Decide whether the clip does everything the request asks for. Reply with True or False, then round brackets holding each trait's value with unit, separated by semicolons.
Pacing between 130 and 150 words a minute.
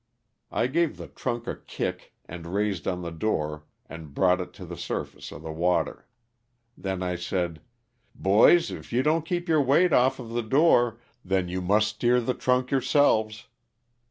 False (175 wpm)